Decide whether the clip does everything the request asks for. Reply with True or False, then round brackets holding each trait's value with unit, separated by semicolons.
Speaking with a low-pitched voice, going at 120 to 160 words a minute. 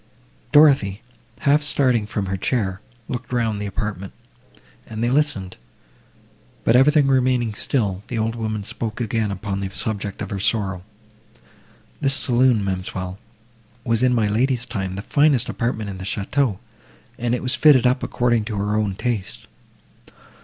True (110 Hz; 150 wpm)